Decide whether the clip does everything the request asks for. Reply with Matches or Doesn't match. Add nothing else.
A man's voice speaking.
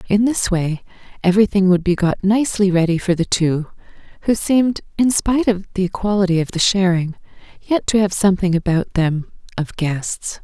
Doesn't match